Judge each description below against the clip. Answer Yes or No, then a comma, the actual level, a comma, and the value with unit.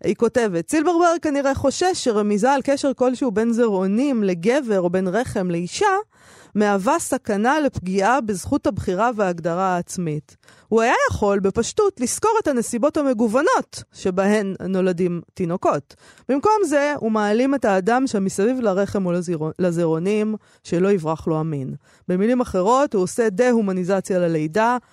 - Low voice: No, high, 215 Hz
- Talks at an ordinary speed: Yes, average, 130 wpm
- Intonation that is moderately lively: No, wide, 6.0 semitones